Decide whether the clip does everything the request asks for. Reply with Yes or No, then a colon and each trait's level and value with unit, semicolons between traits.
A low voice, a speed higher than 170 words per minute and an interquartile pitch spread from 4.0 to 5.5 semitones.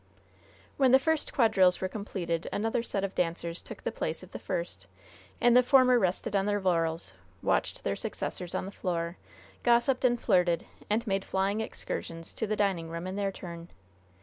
No: high, 195 Hz; average, 180 wpm; average, 5.0 semitones